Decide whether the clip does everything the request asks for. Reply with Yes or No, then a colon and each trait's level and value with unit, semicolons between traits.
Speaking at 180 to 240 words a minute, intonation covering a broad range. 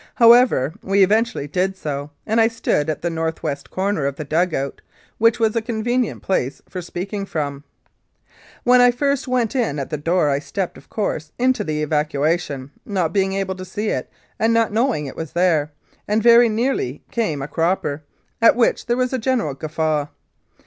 Yes: average, 195 wpm; wide, 7.1 semitones